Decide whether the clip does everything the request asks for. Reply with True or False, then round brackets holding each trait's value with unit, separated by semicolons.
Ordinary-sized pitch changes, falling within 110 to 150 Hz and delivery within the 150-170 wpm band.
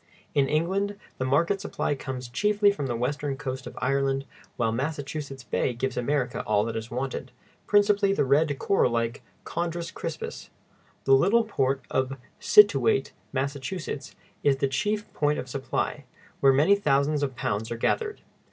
True (4.6 semitones; 140 Hz; 155 wpm)